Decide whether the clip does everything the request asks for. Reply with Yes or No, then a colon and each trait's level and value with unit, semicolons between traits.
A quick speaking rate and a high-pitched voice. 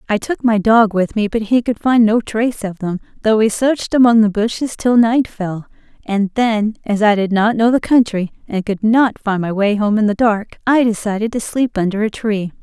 Yes: fast, 235 wpm; high, 215 Hz